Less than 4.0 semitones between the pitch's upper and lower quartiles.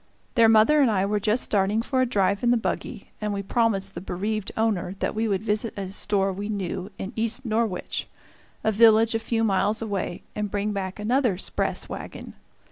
Yes: narrow, 2.4 semitones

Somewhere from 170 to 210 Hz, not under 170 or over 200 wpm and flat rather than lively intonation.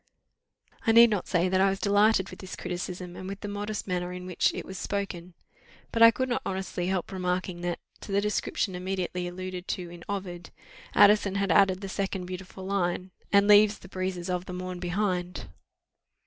Yes: medium, 185 Hz; average, 190 wpm; narrow, 1.9 semitones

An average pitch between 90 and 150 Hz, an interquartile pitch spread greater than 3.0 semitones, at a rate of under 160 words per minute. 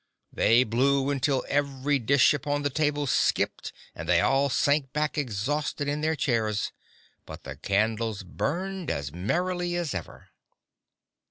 Yes: medium, 140 Hz; average, 4.9 semitones; average, 140 wpm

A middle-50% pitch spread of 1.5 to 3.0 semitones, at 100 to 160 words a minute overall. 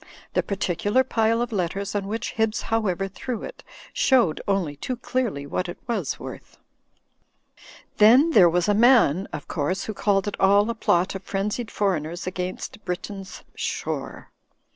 No: average, 3.7 semitones; average, 155 wpm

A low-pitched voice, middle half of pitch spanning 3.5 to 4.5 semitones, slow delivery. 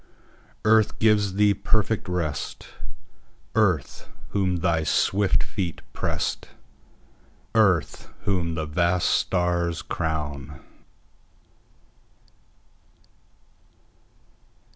Yes: very low, 90 Hz; average, 3.8 semitones; slow, 60 wpm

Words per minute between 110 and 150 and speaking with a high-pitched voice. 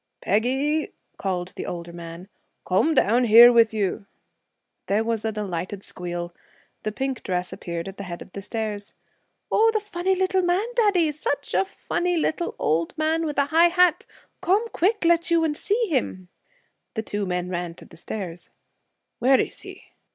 No: average, 175 wpm; high, 230 Hz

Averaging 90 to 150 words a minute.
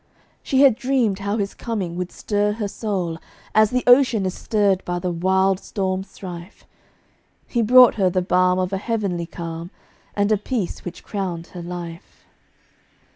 No: average, 165 wpm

